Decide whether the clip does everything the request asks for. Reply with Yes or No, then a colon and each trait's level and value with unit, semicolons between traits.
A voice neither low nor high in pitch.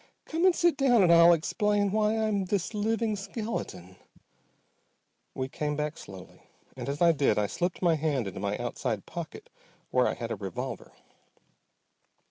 Yes: medium, 175 Hz